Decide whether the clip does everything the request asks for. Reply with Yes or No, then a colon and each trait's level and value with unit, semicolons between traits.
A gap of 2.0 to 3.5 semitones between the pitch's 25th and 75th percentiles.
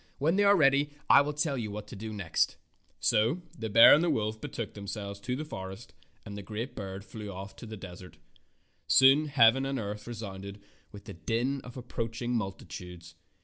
No: average, 4.9 semitones